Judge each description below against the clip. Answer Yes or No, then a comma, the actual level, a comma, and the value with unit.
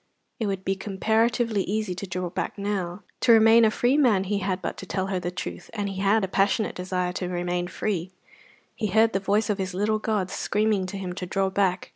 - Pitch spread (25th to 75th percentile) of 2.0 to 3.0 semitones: Yes, average, 2.7 semitones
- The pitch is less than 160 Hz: No, high, 195 Hz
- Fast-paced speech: Yes, fast, 225 wpm